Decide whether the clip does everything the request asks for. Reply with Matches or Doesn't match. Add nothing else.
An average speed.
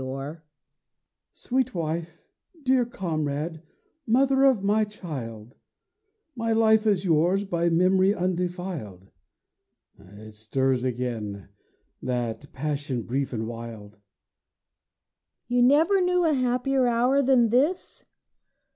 Doesn't match